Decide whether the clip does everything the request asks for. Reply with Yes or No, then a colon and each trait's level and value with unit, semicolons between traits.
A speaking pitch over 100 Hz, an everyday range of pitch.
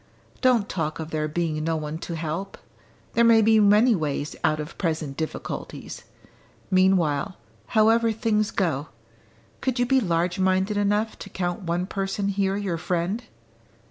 Yes: medium, 185 Hz; average, 4.7 semitones